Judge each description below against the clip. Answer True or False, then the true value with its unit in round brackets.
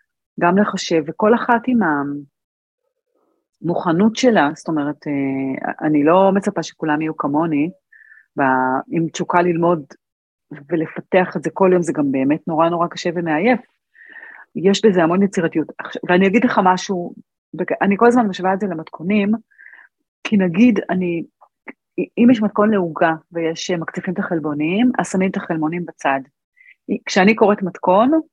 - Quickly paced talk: False (140 wpm)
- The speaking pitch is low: False (180 Hz)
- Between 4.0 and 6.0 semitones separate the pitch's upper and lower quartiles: True (4.5 semitones)